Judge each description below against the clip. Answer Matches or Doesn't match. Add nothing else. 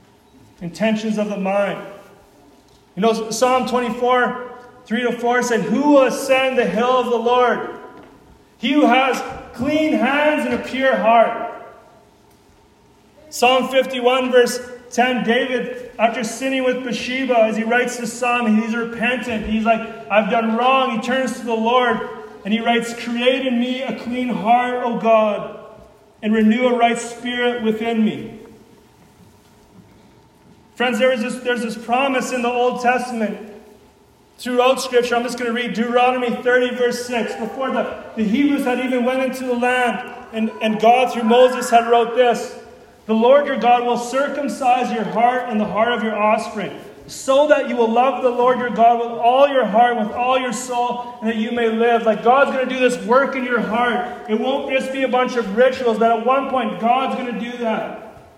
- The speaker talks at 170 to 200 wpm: Matches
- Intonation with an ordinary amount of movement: Doesn't match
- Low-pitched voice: Doesn't match